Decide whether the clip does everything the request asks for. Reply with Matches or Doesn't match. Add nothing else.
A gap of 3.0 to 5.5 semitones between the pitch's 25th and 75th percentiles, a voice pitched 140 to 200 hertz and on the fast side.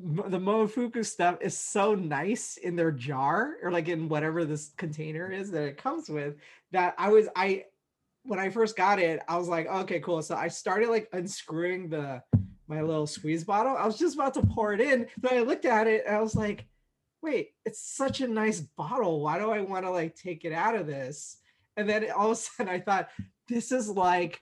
Matches